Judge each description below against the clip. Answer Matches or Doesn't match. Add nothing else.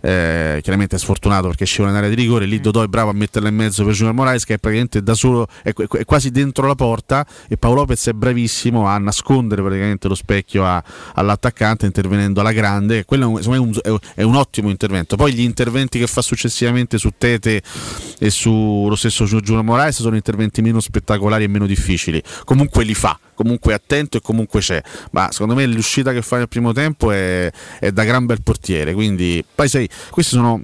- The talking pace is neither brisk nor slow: Doesn't match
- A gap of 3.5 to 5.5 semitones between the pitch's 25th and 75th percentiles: Doesn't match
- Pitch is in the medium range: Doesn't match